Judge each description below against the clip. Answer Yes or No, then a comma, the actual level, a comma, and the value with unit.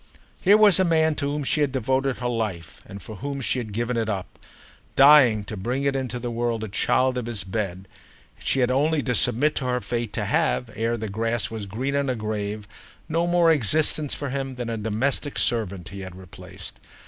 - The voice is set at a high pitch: No, low, 120 Hz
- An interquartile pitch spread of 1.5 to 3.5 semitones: No, average, 4.6 semitones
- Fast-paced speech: Yes, fast, 215 wpm